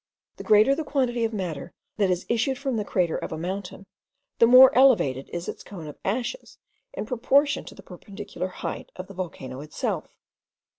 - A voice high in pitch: Yes, high, 205 Hz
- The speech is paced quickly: No, average, 185 wpm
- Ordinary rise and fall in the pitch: No, wide, 5.8 semitones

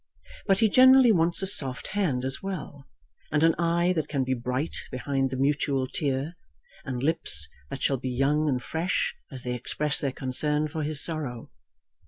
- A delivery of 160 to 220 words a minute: Yes, average, 180 wpm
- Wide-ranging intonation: No, average, 4.0 semitones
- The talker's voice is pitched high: No, medium, 145 Hz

